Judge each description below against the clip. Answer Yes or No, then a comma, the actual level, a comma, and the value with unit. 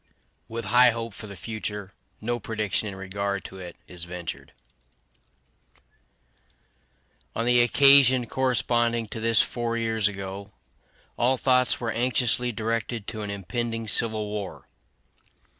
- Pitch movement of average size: Yes, average, 3.0 semitones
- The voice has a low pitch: Yes, low, 115 Hz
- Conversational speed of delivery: No, slow, 125 wpm